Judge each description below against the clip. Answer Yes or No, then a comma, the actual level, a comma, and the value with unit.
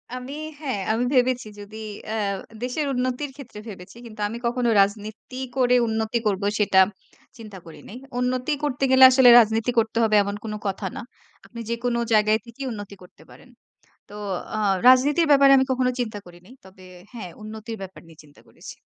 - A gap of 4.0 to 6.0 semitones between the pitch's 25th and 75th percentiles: No, average, 3.4 semitones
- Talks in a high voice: Yes, high, 230 Hz